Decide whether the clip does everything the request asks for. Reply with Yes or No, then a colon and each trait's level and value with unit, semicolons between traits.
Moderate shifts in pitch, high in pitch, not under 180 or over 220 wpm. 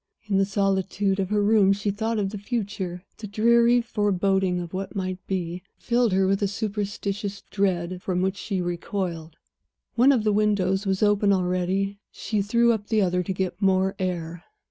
No: narrow, 2.0 semitones; high, 195 Hz; average, 185 wpm